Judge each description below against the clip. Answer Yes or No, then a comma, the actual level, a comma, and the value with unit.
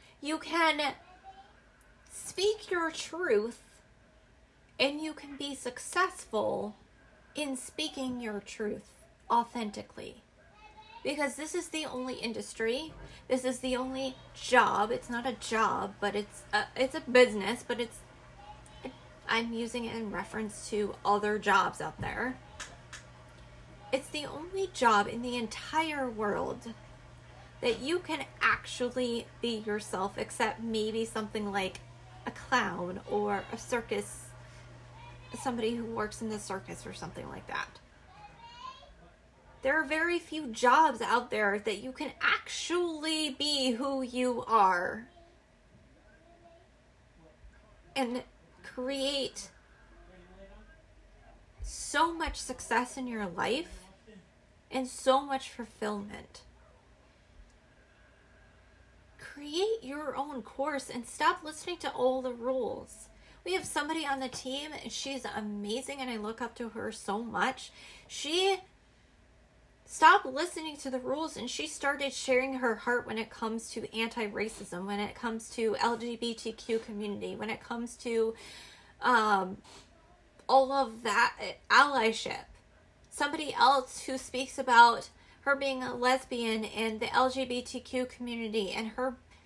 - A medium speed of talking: No, slow, 125 wpm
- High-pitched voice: Yes, very high, 250 Hz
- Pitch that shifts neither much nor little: Yes, average, 4.1 semitones